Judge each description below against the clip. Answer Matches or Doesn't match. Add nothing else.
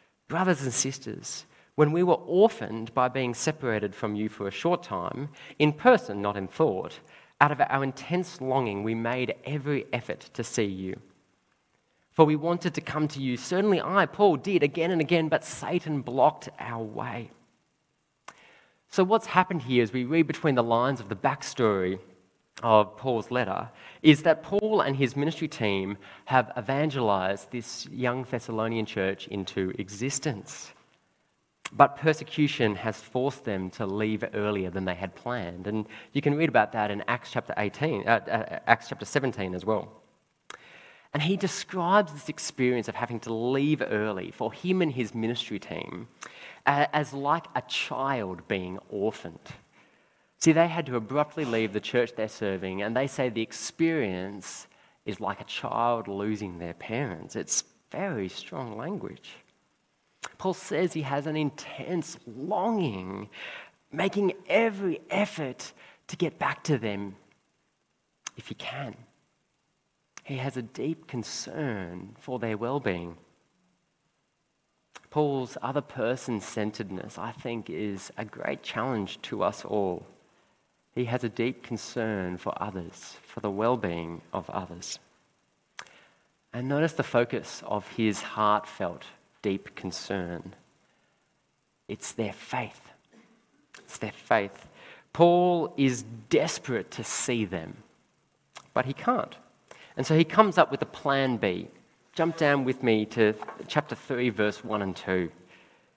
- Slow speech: Doesn't match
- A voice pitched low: Matches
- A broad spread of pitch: Matches